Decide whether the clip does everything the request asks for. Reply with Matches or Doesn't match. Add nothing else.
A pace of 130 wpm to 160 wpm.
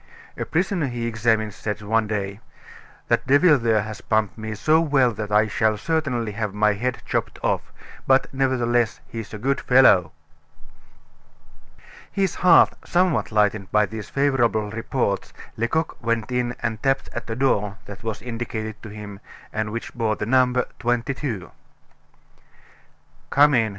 Matches